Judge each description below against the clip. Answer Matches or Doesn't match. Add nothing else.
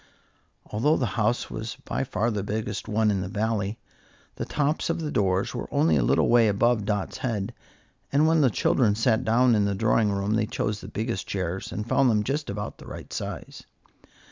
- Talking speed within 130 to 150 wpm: Doesn't match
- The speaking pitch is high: Doesn't match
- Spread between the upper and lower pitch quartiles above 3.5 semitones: Doesn't match